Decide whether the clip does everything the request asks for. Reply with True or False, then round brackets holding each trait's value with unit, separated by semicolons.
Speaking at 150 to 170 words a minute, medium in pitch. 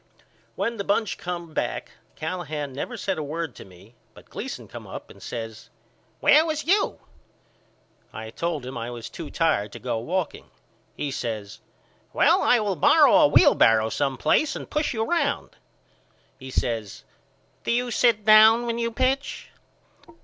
True (160 wpm; 175 Hz)